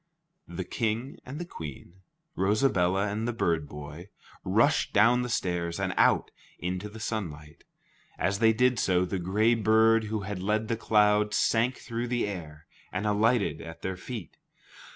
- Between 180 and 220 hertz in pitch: No, low, 105 Hz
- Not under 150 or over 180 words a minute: Yes, average, 160 wpm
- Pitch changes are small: No, average, 3.8 semitones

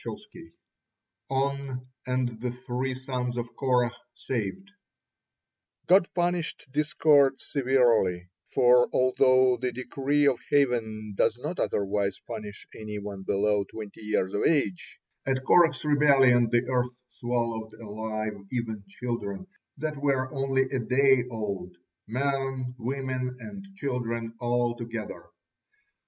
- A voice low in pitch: Yes, low, 125 Hz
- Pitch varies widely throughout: No, average, 3.4 semitones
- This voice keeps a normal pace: No, slow, 115 wpm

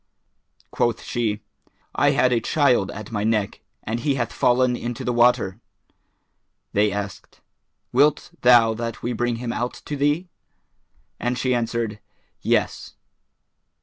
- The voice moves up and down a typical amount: No, narrow, 2.0 semitones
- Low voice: Yes, low, 120 Hz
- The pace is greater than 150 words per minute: No, slow, 135 wpm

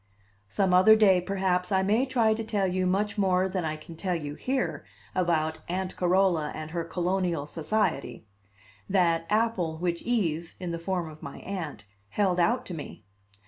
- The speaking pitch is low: No, medium, 180 Hz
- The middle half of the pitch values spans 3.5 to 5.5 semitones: No, average, 3.0 semitones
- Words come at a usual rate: Yes, average, 175 wpm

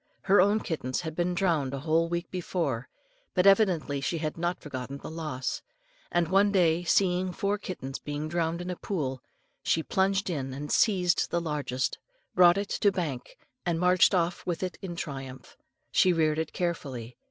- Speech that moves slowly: No, average, 175 wpm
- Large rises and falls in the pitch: No, average, 3.8 semitones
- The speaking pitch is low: No, medium, 170 Hz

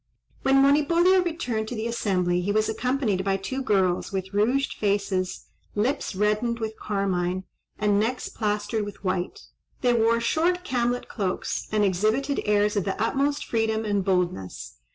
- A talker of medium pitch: No, high, 215 Hz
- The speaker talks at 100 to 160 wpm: Yes, average, 155 wpm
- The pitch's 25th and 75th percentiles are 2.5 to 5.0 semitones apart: Yes, average, 4.0 semitones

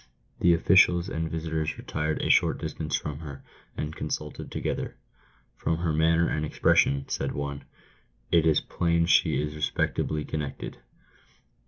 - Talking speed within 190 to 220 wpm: No, average, 150 wpm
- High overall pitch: No, very low, 80 Hz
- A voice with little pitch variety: Yes, narrow, 1.7 semitones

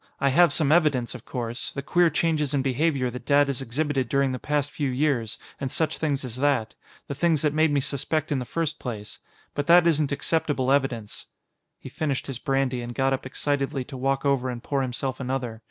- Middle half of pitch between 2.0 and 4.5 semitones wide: Yes, narrow, 2.6 semitones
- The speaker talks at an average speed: No, fast, 210 wpm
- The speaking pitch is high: No, medium, 140 Hz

